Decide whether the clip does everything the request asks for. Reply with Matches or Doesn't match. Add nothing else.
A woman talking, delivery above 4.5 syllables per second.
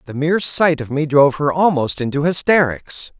Doesn't match